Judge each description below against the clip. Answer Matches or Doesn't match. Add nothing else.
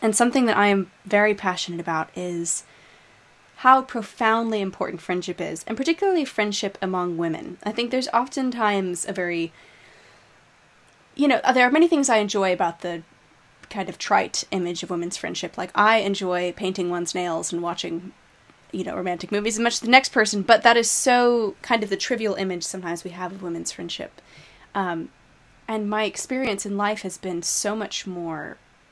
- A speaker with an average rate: Matches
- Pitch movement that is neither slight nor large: Matches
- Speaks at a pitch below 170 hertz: Doesn't match